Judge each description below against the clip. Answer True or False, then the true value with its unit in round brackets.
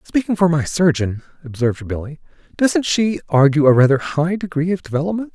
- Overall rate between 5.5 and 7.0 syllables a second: True (5.6 syllables/s)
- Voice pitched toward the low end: False (160 Hz)